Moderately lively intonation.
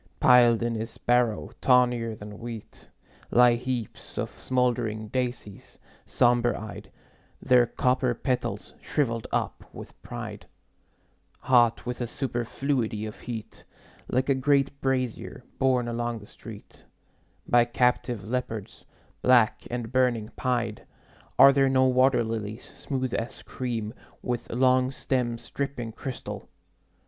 No: narrow, 1.8 semitones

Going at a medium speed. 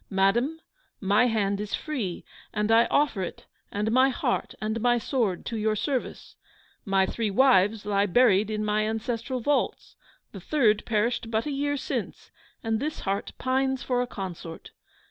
Yes: average, 165 wpm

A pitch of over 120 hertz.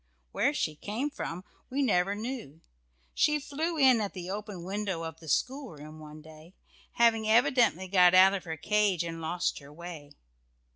Yes: high, 190 Hz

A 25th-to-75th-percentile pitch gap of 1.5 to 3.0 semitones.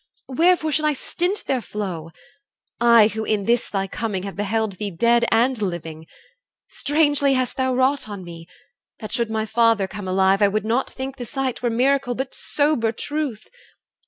No: average, 4.6 semitones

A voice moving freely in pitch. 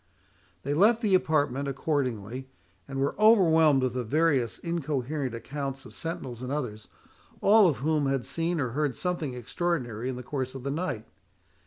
No: average, 4.2 semitones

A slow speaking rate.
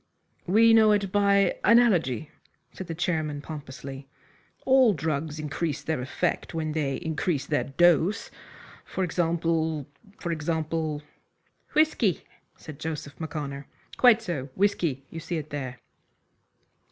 Yes: slow, 125 wpm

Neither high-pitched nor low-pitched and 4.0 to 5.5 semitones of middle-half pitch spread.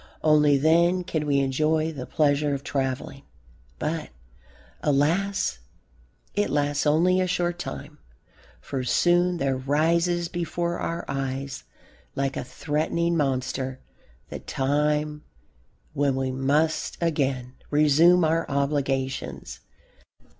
No: medium, 150 Hz; average, 3.5 semitones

